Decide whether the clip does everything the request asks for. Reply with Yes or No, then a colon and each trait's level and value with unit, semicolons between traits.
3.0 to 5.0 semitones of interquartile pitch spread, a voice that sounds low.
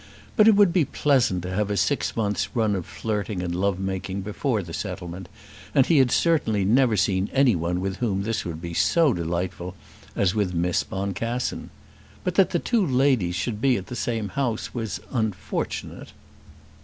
No: wide, 5.4 semitones; low, 105 Hz